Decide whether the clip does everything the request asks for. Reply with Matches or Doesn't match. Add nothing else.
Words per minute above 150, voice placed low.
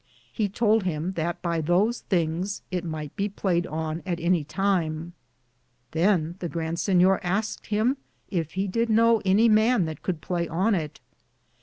Doesn't match